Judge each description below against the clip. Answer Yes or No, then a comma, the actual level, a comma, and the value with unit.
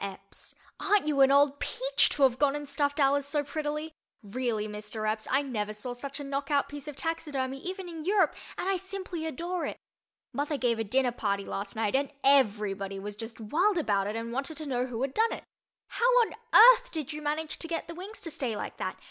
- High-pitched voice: Yes, very high, 280 Hz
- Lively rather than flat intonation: Yes, wide, 5.8 semitones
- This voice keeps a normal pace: No, fast, 220 wpm